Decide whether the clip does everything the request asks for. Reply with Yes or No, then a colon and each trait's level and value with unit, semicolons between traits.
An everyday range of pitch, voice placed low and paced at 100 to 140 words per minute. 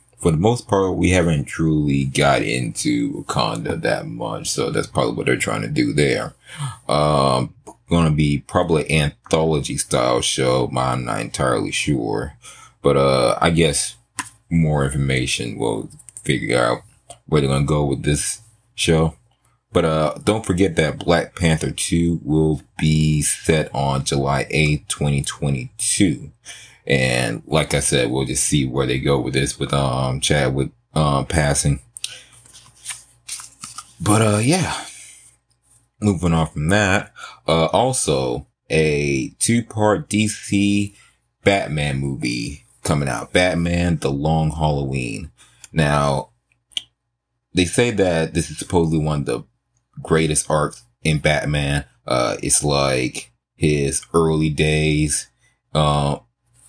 No: wide, 6.0 semitones; very low, 80 Hz; slow, 135 wpm